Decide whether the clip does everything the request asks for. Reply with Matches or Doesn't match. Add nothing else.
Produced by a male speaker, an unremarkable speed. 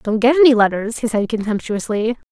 Doesn't match